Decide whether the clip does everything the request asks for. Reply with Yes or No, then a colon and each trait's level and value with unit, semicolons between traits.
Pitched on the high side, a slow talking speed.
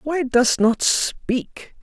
Yes: very high, 260 Hz; slow, 130 wpm